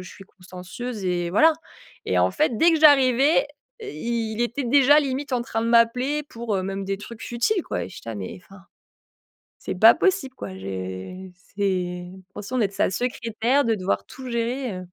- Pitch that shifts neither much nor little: No, wide, 5.7 semitones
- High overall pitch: Yes, high, 230 Hz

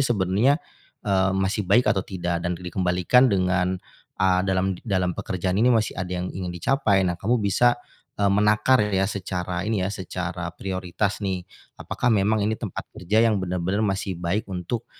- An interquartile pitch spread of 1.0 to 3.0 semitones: Yes, narrow, 2.5 semitones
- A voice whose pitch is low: Yes, very low, 95 Hz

